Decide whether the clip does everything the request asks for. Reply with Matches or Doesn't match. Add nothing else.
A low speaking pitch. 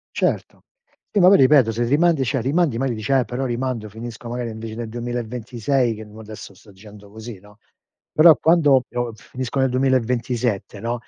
Matches